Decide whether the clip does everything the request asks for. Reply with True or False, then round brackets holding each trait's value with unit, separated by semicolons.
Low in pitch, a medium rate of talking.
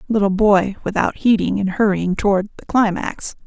False (200 Hz; 155 wpm)